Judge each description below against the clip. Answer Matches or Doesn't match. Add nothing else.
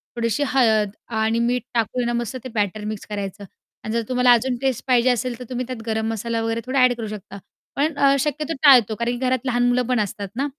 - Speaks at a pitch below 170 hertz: Doesn't match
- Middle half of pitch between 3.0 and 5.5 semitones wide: Doesn't match